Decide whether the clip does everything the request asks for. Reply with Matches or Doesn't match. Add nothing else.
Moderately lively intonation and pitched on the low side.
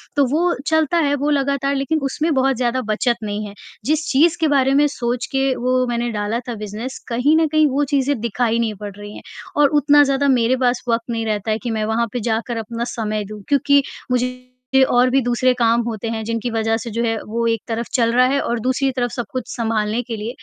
Doesn't match